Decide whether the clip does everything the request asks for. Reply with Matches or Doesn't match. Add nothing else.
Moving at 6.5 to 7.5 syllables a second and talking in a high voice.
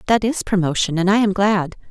Doesn't match